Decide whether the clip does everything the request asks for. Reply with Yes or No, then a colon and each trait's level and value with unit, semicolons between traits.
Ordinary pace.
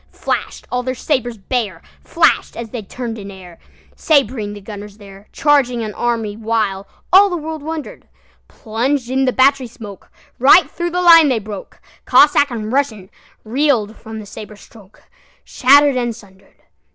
No: slow, 125 wpm